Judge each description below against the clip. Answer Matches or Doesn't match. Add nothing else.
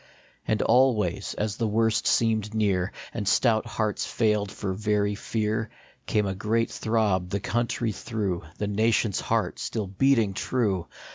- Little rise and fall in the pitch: Matches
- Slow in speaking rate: Doesn't match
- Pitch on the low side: Matches